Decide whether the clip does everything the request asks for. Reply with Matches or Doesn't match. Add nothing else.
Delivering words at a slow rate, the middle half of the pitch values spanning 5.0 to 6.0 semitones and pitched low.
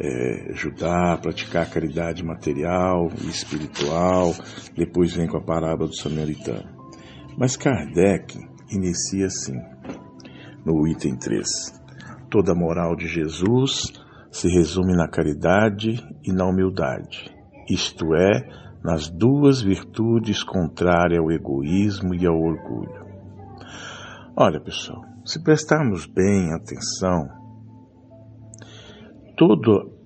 Matches